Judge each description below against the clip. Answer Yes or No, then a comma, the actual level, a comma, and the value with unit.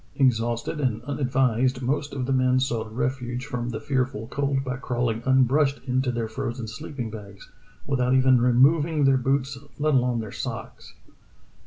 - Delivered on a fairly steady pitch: Yes, narrow, 2.2 semitones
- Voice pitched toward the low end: Yes, low, 125 Hz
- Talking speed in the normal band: Yes, average, 160 wpm